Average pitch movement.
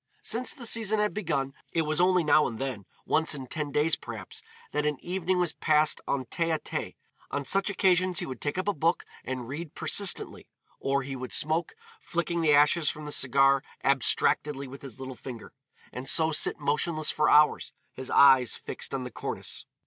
Yes: average, 4.0 semitones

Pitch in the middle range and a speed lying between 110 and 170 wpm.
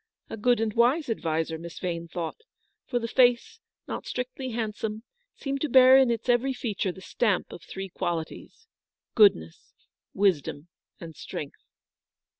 No: high, 220 Hz; average, 155 wpm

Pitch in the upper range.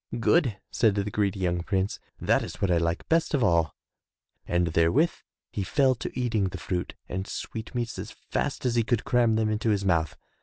No: low, 105 Hz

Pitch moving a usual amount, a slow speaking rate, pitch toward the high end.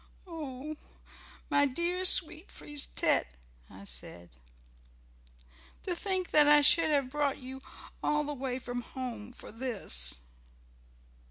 Yes: average, 3.9 semitones; slow, 120 wpm; very high, 280 Hz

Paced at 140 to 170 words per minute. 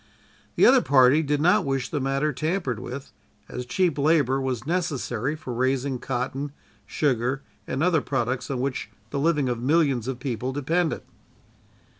Yes: average, 155 wpm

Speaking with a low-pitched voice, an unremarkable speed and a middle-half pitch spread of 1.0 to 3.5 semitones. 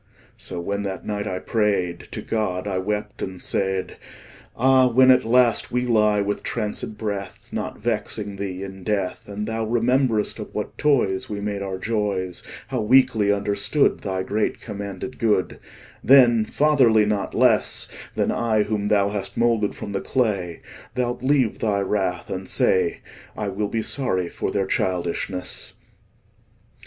Yes: low, 105 Hz; average, 160 wpm; average, 2.9 semitones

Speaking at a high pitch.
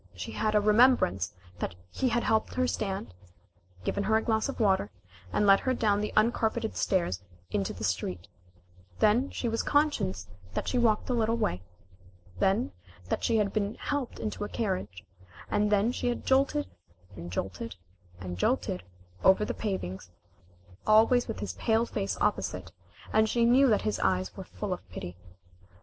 Yes: high, 210 Hz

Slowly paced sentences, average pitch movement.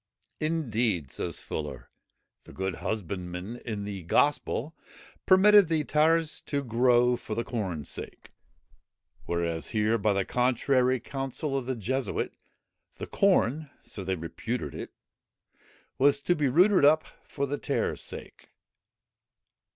No: slow, 130 wpm; wide, 6.3 semitones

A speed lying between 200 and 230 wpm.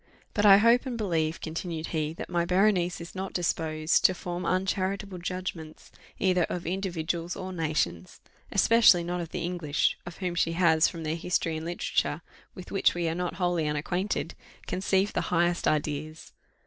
No: average, 170 wpm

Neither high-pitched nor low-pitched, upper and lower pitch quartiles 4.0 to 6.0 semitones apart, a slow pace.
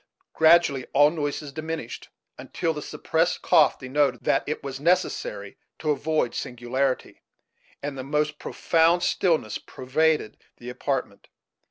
No: medium, 150 Hz; average, 3.3 semitones; slow, 125 wpm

